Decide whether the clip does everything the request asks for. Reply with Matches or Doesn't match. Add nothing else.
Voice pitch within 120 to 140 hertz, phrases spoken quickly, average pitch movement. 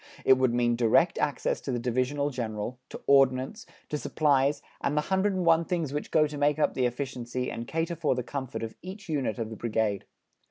Matches